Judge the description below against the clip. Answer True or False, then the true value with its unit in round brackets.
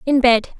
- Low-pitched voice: False (250 Hz)